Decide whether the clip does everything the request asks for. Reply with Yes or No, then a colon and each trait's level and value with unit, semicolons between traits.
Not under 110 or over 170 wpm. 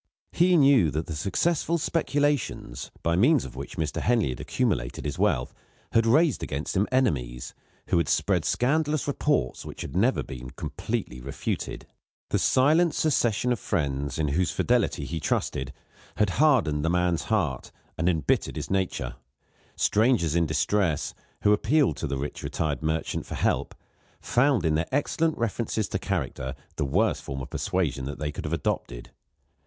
Yes: average, 160 wpm